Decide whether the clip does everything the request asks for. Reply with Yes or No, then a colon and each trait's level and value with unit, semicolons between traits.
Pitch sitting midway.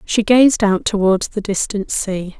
No: high, 205 Hz